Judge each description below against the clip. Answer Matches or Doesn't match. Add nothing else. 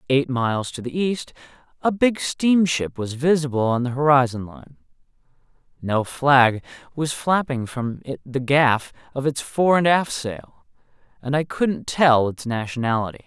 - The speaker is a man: Matches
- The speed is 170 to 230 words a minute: Doesn't match